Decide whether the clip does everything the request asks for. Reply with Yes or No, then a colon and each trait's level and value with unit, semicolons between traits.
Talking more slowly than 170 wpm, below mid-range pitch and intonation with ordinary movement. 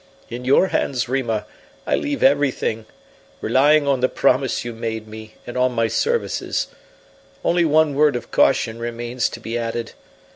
Yes: average, 155 wpm; low, 125 Hz; average, 3.6 semitones